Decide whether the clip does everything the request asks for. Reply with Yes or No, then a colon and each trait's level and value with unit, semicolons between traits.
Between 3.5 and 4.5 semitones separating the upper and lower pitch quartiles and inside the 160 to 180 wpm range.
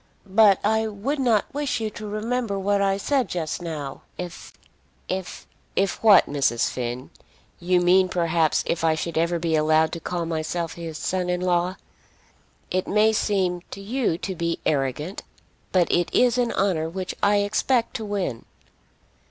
Yes: average, 3.9 semitones; average, 170 wpm